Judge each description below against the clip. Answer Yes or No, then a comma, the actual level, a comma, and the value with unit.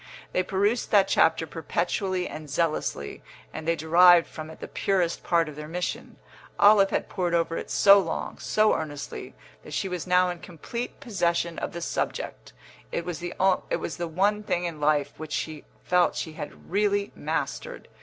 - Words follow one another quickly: No, average, 170 wpm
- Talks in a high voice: No, medium, 175 Hz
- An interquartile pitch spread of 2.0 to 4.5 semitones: Yes, average, 3.1 semitones